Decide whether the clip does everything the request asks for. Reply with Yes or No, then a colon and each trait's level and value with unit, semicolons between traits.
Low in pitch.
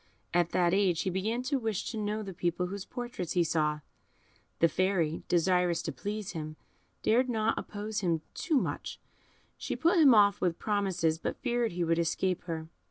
No: medium, 185 Hz